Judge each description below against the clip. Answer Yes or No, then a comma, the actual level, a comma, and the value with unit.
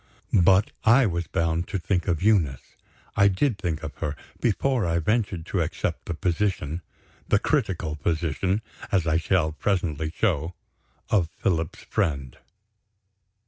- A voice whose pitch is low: Yes, very low, 85 Hz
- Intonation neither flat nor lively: Yes, average, 3.7 semitones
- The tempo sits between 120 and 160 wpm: Yes, average, 140 wpm